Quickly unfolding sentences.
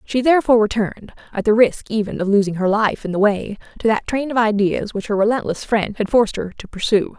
Yes: fast, 235 wpm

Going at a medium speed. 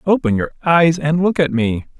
No: fast, 210 wpm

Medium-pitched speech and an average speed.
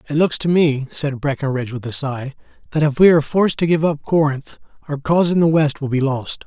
No: medium, 145 Hz; fast, 240 wpm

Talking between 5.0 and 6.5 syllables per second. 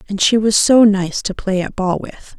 No: 4.7 syllables/s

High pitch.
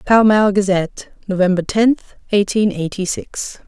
Yes: high, 200 Hz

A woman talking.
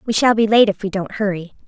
Yes: female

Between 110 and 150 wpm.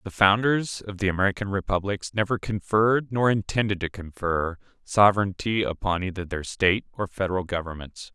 Yes: average, 145 wpm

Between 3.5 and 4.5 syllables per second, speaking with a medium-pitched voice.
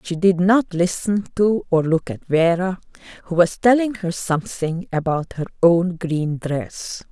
Yes: 4.0 syllables/s; medium, 175 Hz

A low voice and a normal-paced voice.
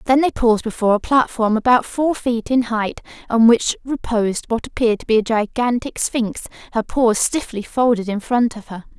No: high, 230 Hz; average, 195 wpm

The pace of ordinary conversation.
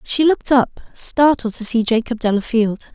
Yes: average, 165 wpm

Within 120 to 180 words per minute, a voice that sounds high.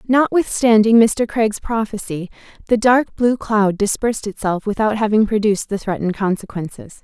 Yes: slow, 135 wpm; high, 215 Hz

